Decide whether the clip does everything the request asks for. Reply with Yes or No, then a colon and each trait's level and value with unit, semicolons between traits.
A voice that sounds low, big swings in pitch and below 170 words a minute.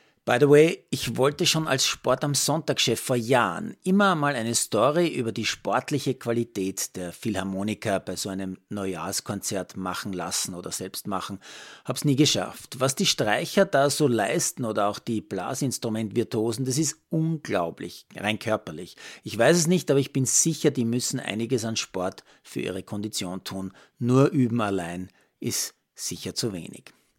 Yes: low, 120 Hz; wide, 6.0 semitones; average, 160 wpm